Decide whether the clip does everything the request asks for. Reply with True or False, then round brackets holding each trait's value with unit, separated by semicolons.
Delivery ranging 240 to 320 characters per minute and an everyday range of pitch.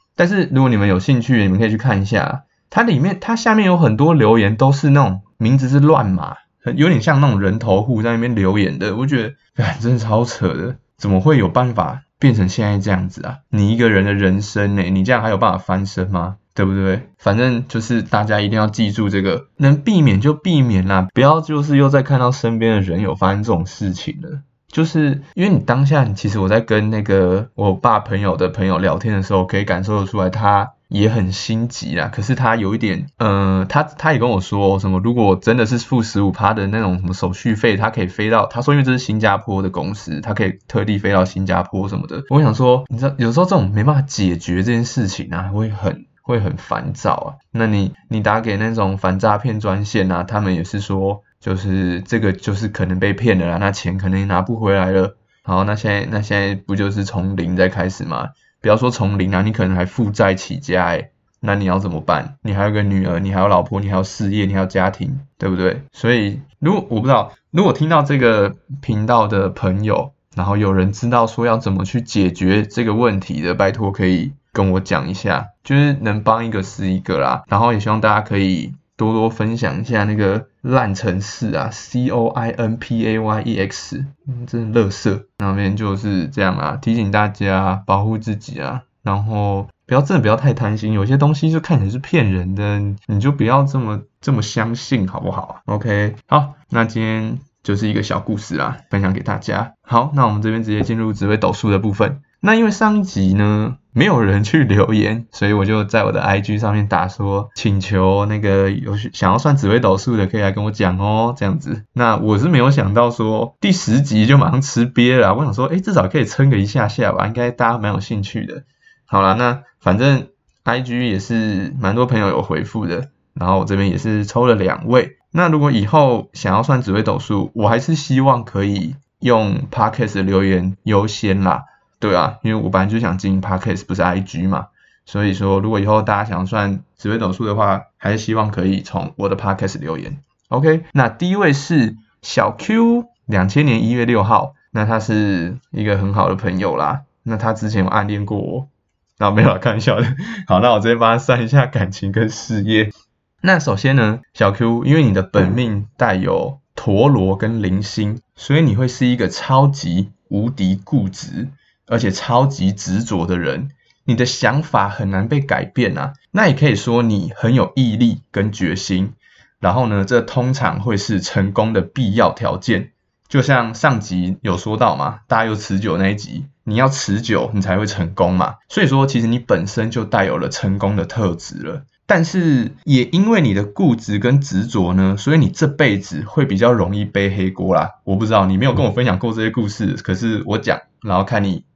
True (310 characters per minute; 4.3 semitones)